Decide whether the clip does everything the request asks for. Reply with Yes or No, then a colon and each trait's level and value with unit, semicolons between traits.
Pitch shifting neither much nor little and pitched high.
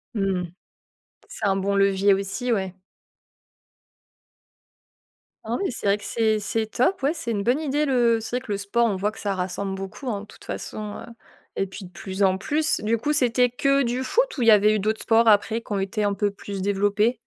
Yes: average, 3.3 semitones; high, 215 Hz